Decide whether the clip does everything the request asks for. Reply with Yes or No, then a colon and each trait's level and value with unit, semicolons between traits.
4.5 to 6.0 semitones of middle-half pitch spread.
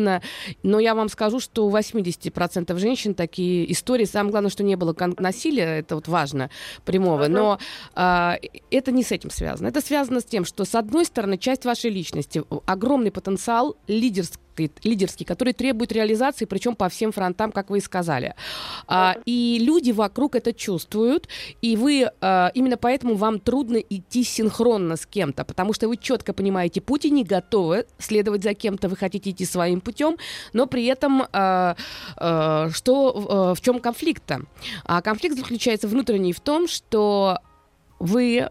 Yes: average, 4.8 semitones